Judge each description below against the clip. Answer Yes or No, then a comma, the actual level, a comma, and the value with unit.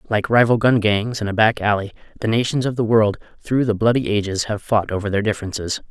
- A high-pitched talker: No, low, 110 Hz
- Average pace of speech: No, fast, 225 wpm